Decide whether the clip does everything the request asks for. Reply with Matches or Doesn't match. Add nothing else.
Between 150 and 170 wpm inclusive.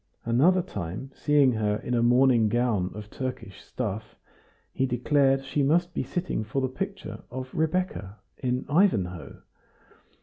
Doesn't match